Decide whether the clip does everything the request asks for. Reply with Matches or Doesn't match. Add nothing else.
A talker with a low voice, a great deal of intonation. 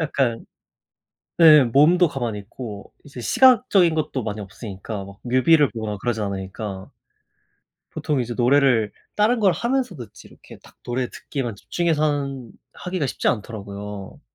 Matches